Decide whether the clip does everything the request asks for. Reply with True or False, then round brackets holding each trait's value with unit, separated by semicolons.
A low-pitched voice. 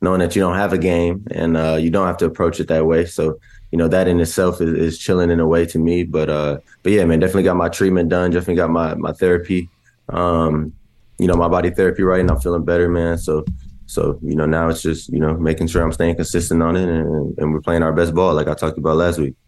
True (85 Hz)